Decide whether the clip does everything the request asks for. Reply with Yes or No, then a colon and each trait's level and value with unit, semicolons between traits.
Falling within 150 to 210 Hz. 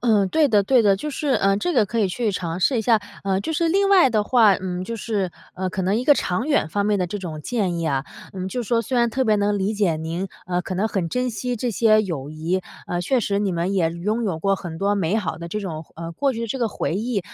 Yes: high, 200 Hz